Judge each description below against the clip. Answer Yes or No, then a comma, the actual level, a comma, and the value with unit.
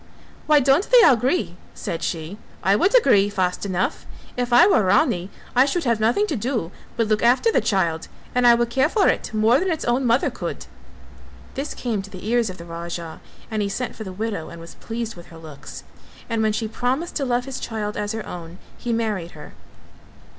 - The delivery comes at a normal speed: No, fast, 210 wpm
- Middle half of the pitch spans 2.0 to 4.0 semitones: No, average, 5.1 semitones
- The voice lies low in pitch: No, high, 220 Hz